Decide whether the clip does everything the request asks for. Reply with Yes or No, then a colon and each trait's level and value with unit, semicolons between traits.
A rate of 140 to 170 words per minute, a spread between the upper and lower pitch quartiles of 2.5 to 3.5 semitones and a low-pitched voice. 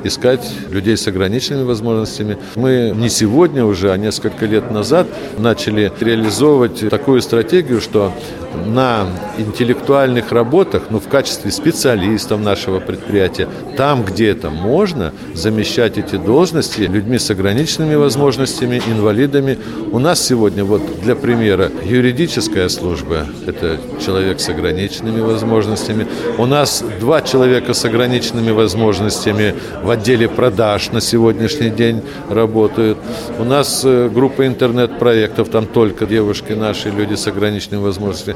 No: average, 120 wpm; average, 2.9 semitones; low, 110 Hz